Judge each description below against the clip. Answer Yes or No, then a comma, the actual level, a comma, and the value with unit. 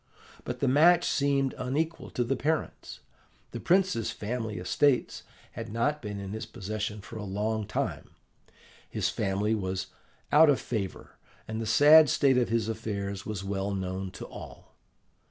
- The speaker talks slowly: No, average, 155 wpm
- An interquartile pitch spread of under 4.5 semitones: No, wide, 5.5 semitones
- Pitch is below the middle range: Yes, low, 110 Hz